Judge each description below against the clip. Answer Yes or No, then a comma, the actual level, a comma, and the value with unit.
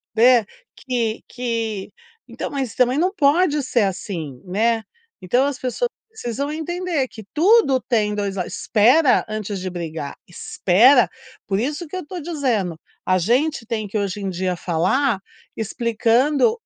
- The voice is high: Yes, high, 235 Hz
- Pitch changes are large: Yes, wide, 6.3 semitones